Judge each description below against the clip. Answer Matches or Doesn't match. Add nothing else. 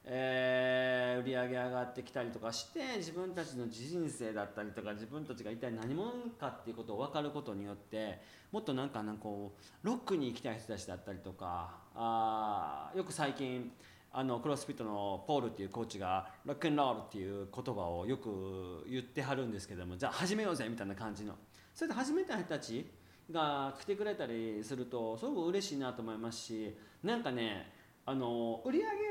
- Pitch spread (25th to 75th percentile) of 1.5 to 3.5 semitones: Doesn't match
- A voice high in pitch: Doesn't match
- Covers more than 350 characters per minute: Matches